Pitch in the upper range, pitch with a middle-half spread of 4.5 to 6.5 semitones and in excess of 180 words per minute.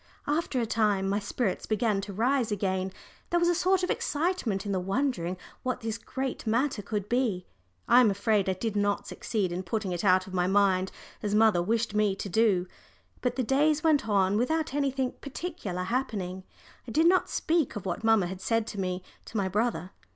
Yes: high, 215 Hz; average, 5.1 semitones; average, 200 wpm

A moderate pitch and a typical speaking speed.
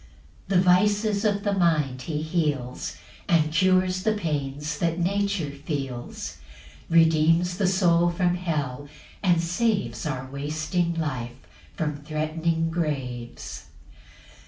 No: medium, 165 Hz; slow, 115 wpm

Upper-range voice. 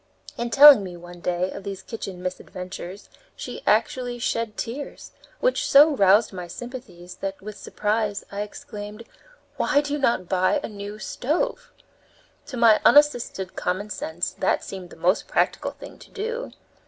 Yes: high, 210 Hz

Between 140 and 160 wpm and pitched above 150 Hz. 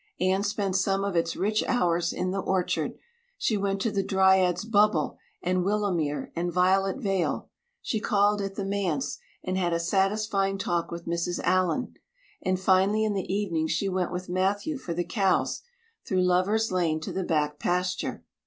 No: average, 170 wpm; high, 190 Hz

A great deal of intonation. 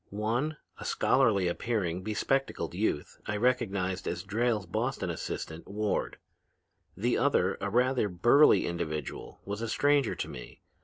No: average, 4.9 semitones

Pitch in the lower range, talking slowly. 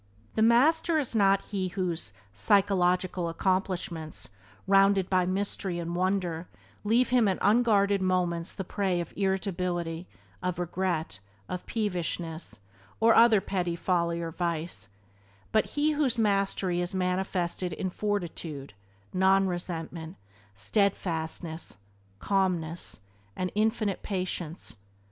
No: medium, 185 Hz; slow, 110 wpm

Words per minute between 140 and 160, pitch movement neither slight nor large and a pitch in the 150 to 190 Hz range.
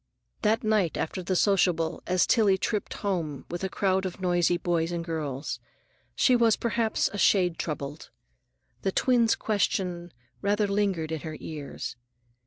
Yes: average, 150 wpm; average, 3.8 semitones; medium, 185 Hz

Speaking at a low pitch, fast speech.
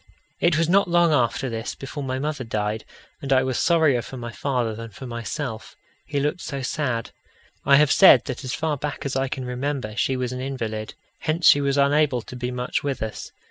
Yes: low, 130 Hz; fast, 215 wpm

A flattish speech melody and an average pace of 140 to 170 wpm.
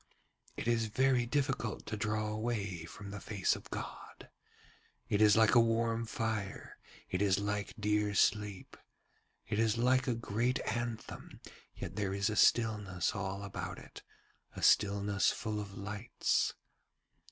Yes: narrow, 2.1 semitones; average, 145 wpm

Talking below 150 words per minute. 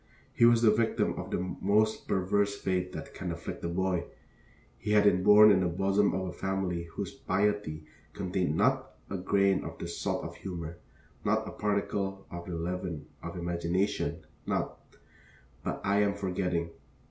No: average, 170 wpm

